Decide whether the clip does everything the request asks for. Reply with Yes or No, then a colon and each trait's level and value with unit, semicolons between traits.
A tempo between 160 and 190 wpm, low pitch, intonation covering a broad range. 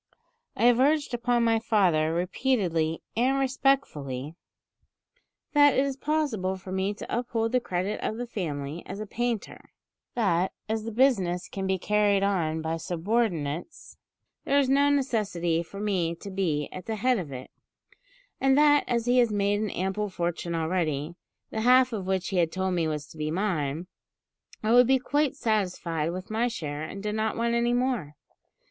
No: average, 175 wpm; high, 200 Hz; wide, 6.0 semitones